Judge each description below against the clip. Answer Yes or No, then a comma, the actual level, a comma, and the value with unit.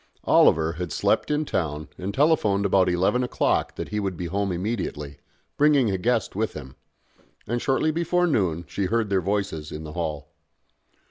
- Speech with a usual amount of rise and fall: No, wide, 6.0 semitones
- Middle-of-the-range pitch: No, low, 100 Hz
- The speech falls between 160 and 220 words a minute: Yes, average, 175 wpm